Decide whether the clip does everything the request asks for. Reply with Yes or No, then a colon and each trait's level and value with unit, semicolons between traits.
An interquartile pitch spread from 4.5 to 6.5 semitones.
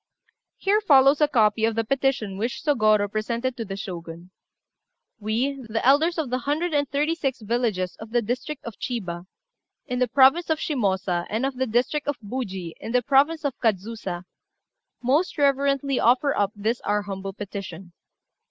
Yes: average, 5.2 semitones